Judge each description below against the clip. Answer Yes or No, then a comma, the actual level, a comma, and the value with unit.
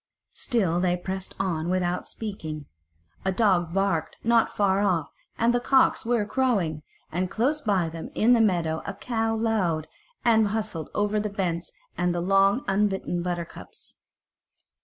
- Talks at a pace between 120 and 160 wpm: Yes, average, 155 wpm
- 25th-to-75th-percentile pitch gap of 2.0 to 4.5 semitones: Yes, average, 4.1 semitones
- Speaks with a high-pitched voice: Yes, high, 195 Hz